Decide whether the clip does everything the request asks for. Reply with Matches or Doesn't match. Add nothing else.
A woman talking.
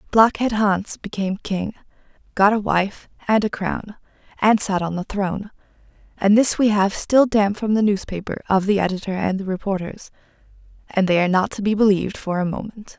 Matches